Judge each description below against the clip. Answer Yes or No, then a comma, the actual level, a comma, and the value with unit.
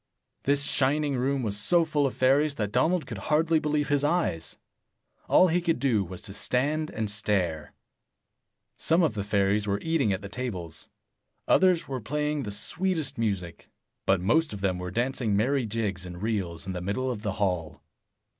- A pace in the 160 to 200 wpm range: Yes, average, 185 wpm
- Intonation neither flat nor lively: No, wide, 6.9 semitones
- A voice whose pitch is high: No, low, 120 Hz